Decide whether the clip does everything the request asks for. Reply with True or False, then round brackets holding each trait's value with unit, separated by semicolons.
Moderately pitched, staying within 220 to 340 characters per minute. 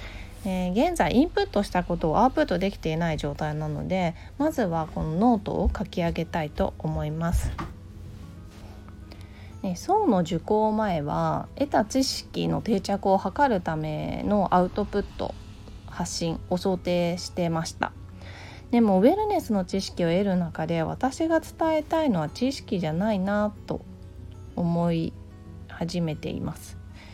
True (170 Hz; 290 characters per minute)